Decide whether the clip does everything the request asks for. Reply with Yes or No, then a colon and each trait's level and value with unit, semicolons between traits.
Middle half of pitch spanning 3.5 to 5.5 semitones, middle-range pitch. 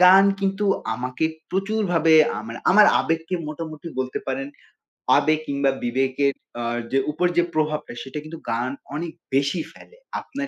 Yes: average, 5.0 semitones; medium, 155 Hz